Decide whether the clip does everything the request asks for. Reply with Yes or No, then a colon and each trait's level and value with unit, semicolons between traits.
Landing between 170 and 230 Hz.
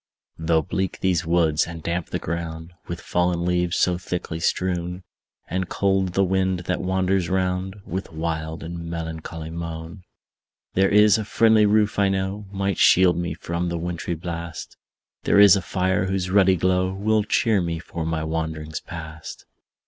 No: very low, 90 Hz